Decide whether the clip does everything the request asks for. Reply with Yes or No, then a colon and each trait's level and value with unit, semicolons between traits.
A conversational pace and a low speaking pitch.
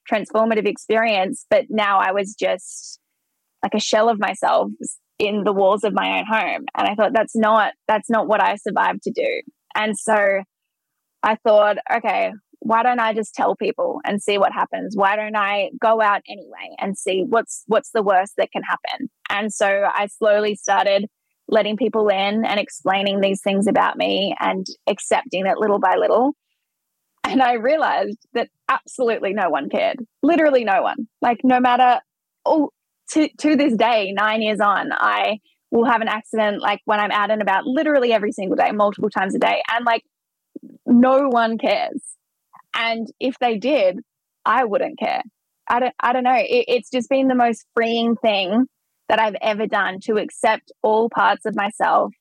No: average, 180 wpm; high, 225 Hz